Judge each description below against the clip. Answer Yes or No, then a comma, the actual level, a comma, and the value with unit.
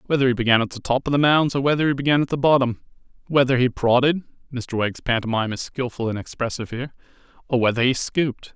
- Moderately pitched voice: No, low, 130 Hz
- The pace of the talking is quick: Yes, fast, 215 wpm